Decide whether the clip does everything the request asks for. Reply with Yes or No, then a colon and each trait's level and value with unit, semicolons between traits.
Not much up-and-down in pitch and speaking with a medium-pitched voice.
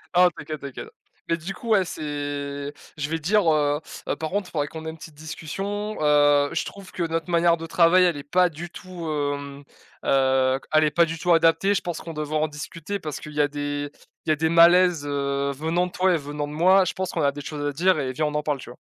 No: average, 3.2 semitones; medium, 155 Hz